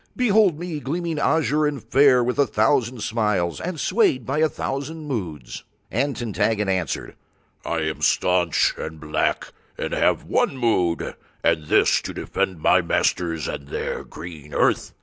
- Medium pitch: No, low, 120 Hz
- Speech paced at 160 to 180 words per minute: No, average, 150 wpm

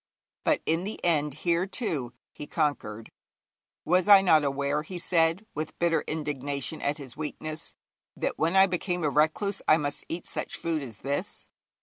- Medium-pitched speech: Yes, medium, 155 Hz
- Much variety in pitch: No, average, 3.4 semitones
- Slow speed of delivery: No, average, 170 wpm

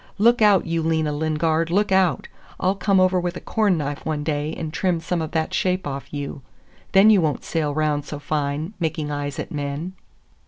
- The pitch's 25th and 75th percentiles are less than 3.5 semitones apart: No, average, 3.8 semitones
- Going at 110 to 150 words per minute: No, fast, 205 wpm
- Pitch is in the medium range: Yes, medium, 160 Hz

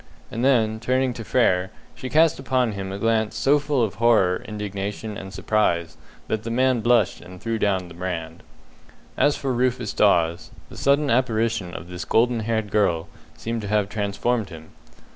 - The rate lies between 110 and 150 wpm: No, average, 175 wpm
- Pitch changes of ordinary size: Yes, average, 4.2 semitones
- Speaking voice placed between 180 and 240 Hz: No, low, 110 Hz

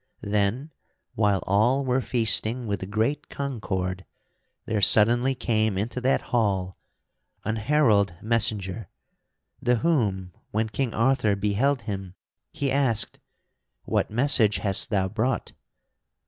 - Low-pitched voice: Yes, low, 110 Hz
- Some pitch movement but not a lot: Yes, average, 3.9 semitones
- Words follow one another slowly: Yes, slow, 115 wpm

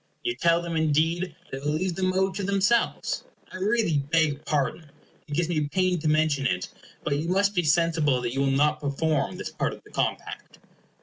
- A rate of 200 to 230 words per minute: Yes, fast, 205 wpm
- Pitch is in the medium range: Yes, medium, 160 Hz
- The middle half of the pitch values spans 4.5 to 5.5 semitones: No, average, 4.0 semitones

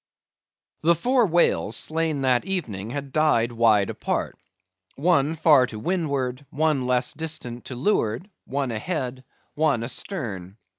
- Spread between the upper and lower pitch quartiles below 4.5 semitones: No, average, 5.0 semitones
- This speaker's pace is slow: Yes, slow, 130 wpm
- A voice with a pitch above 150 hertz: No, medium, 140 Hz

